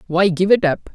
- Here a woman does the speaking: No, male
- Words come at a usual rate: No, fast, 255 wpm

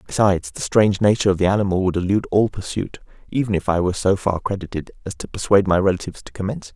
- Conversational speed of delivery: No, fast, 230 wpm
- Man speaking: Yes, male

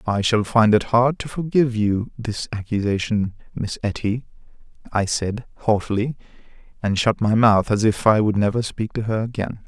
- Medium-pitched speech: No, low, 110 Hz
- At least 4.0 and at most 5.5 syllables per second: Yes, 5.0 syllables/s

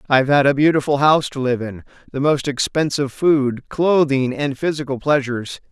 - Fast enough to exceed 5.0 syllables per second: Yes, 5.4 syllables/s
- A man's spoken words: Yes, male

